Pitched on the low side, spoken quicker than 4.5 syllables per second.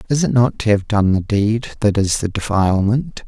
Yes: low, 110 Hz; 5.1 syllables/s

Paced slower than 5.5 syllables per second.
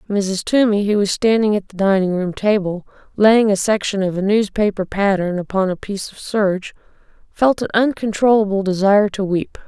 Yes: 5.3 syllables/s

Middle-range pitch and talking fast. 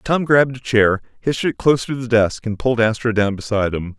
No: low, 115 Hz; fast, 240 wpm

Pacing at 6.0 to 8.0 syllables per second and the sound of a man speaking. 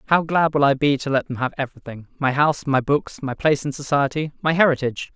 Yes: 6.5 syllables/s; male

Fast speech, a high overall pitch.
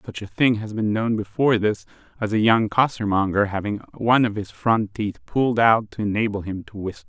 No: fast, 220 wpm; low, 110 Hz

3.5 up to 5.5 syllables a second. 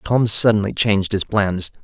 Yes: 4.7 syllables/s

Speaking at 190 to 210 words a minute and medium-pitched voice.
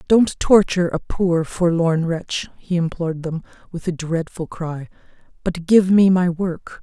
No: average, 160 wpm; medium, 170 Hz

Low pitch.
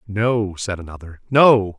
Yes: low, 105 Hz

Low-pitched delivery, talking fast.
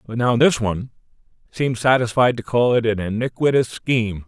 No: low, 120 Hz; average, 170 wpm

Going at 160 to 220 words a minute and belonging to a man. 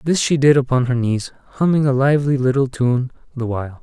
Yes: fast, 205 wpm; male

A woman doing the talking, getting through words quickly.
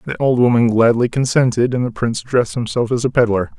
No: male; fast, 220 wpm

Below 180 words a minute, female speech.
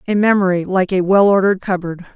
No: average, 195 wpm; female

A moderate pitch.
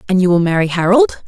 No: high, 195 Hz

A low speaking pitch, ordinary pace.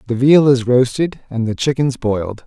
Yes: low, 125 Hz; average, 195 wpm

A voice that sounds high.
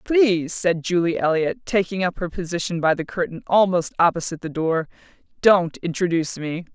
No: medium, 175 Hz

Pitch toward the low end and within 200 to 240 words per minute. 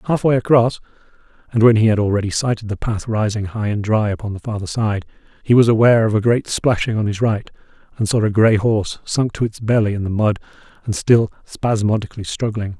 Yes: low, 110 Hz; fast, 205 wpm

